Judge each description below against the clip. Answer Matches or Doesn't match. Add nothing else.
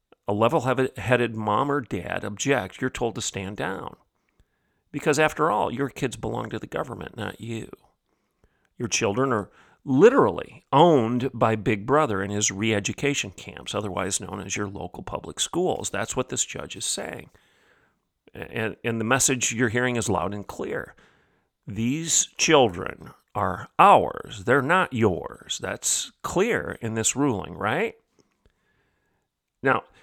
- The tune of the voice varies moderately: Matches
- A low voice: Matches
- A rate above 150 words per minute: Doesn't match